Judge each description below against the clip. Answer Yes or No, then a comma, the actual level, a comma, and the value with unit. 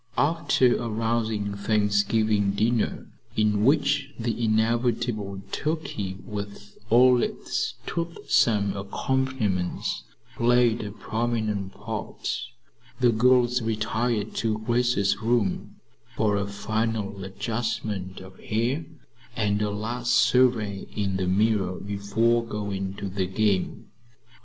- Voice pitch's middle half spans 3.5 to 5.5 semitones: No, average, 2.7 semitones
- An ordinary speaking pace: No, slow, 105 wpm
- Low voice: Yes, low, 110 Hz